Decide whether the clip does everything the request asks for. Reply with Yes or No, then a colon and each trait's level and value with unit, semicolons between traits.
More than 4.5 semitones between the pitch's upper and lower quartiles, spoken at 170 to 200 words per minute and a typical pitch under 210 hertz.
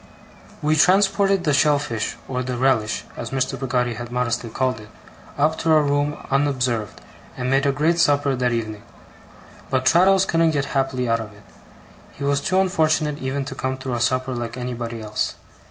No: average, 3.5 semitones; average, 180 wpm; low, 135 Hz